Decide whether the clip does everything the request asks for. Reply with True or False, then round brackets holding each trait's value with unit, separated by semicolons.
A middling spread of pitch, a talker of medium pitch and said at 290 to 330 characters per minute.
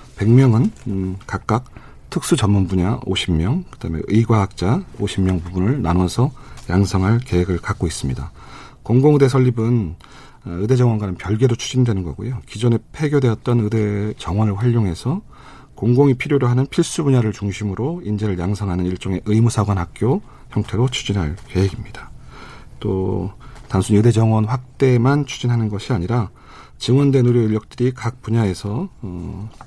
False (4.5 semitones; 110 Hz; 315 characters per minute)